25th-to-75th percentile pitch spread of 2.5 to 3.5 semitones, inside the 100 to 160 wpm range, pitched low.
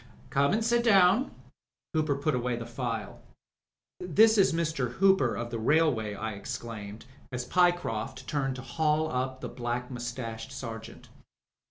No: average, 5.3 semitones; average, 145 wpm; low, 130 Hz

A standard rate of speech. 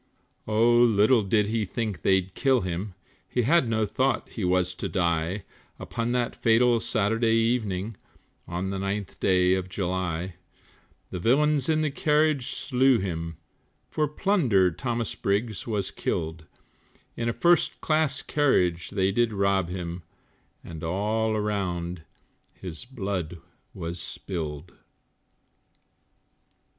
No: slow, 125 wpm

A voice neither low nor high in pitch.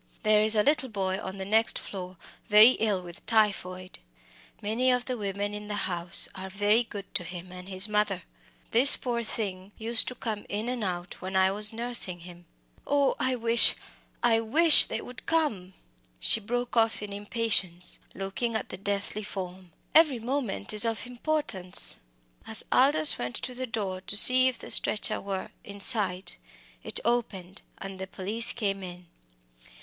No: high, 210 Hz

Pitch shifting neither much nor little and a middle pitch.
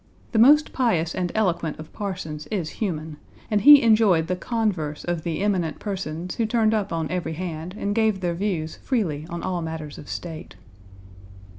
Yes: average, 4.8 semitones; medium, 180 Hz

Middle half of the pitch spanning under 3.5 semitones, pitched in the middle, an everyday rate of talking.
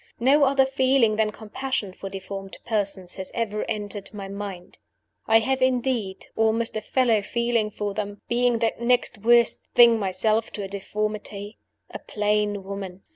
No: average, 3.0 semitones; high, 215 Hz; average, 155 wpm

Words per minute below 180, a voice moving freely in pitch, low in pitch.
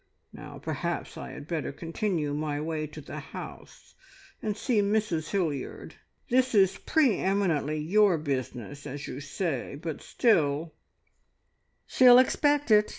No: average, 140 wpm; wide, 6.4 semitones; medium, 165 Hz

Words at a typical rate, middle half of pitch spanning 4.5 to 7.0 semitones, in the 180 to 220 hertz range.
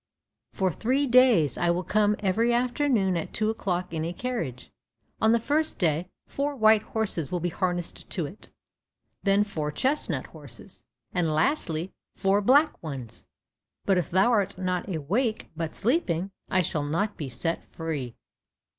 Yes: average, 155 wpm; wide, 5.5 semitones; high, 190 Hz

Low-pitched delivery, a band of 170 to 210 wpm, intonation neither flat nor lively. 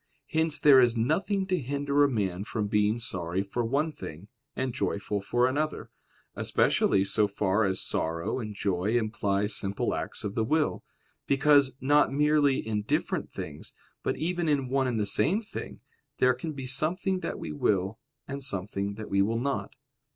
No: low, 120 Hz; average, 175 wpm; wide, 6.1 semitones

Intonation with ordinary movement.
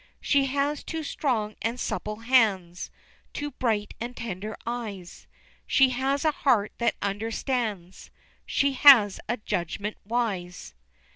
Yes: average, 4.4 semitones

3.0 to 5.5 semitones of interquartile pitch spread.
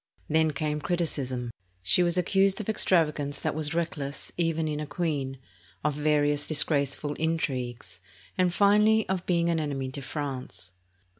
Yes: average, 3.3 semitones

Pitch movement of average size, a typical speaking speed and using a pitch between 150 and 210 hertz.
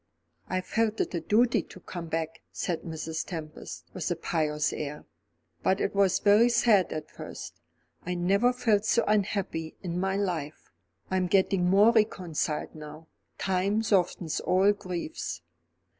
Yes: average, 3.9 semitones; average, 150 wpm; medium, 185 Hz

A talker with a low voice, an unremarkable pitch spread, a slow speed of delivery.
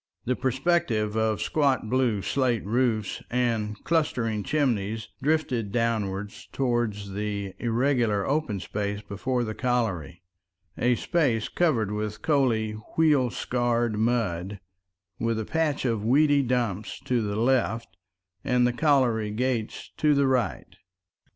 Yes: low, 115 Hz; average, 3.7 semitones; slow, 120 wpm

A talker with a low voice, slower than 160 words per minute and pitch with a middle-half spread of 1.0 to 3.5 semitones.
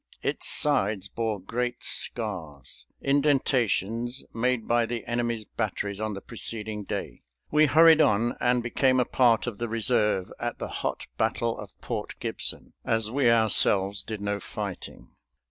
Yes: low, 115 Hz; average, 145 wpm; average, 2.9 semitones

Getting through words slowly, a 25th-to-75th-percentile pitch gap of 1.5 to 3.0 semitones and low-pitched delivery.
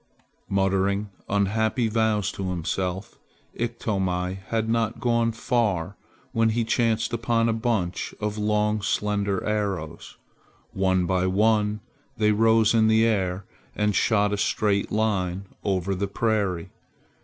Yes: slow, 125 wpm; narrow, 2.6 semitones; low, 105 Hz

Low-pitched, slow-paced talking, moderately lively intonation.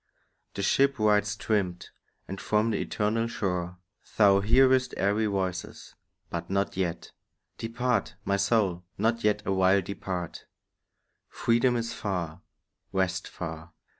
Yes: low, 100 Hz; slow, 120 wpm; average, 3.4 semitones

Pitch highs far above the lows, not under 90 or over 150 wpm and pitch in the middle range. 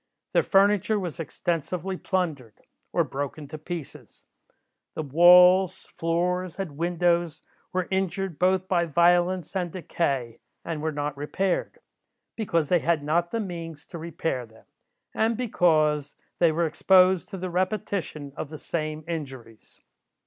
No: average, 3.2 semitones; slow, 135 wpm; medium, 170 Hz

